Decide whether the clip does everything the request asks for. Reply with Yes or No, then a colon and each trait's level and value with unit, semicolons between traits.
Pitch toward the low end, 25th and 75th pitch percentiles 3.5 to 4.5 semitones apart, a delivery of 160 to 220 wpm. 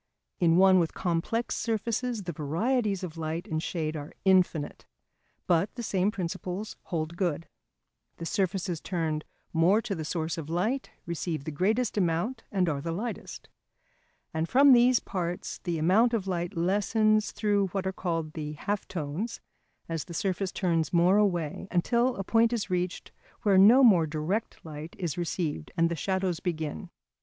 No: medium, 180 Hz; average, 3.9 semitones; average, 165 wpm